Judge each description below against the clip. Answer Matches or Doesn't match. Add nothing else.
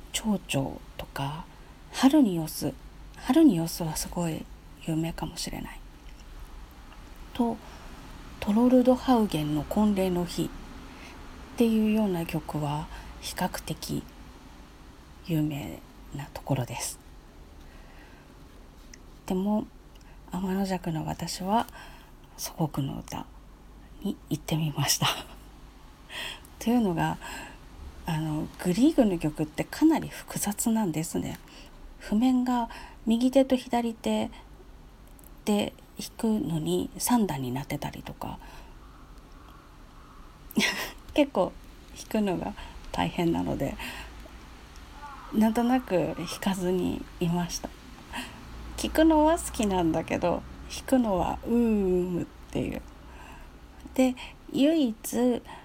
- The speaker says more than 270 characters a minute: Doesn't match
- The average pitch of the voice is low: Doesn't match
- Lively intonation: Matches